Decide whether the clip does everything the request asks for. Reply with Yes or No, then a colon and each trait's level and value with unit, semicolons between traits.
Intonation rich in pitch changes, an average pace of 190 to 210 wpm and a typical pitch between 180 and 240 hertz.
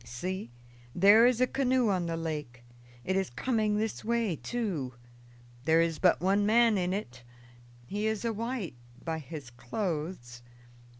No: wide, 6.1 semitones; average, 155 wpm; high, 190 Hz